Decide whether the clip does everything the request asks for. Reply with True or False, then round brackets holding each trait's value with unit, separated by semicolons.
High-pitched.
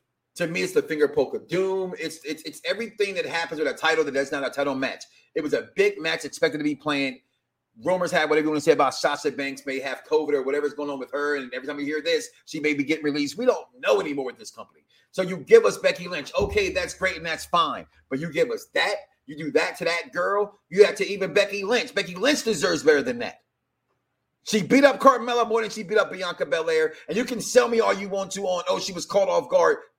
True (195 Hz)